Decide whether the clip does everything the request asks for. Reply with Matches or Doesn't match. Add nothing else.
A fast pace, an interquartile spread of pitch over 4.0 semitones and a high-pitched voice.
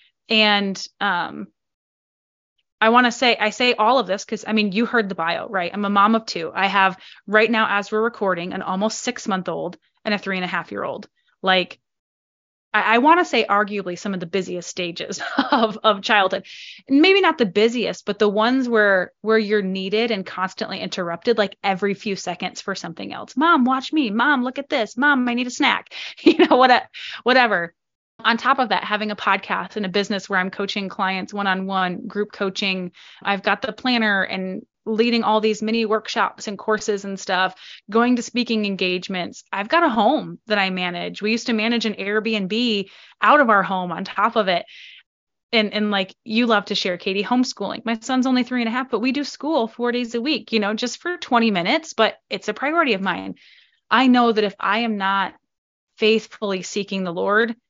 Doesn't match